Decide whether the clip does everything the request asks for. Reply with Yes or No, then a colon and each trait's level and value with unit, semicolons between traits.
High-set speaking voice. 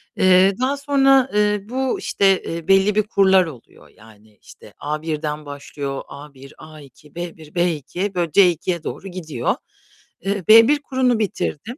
No: medium, 180 Hz